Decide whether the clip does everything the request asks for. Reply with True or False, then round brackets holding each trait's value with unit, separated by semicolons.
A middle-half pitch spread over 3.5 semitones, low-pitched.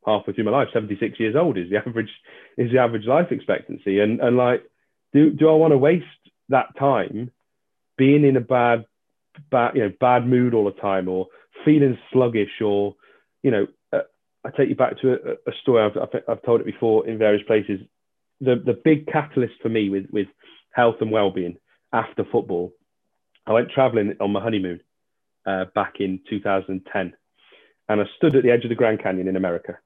True (4.0 semitones; 115 Hz)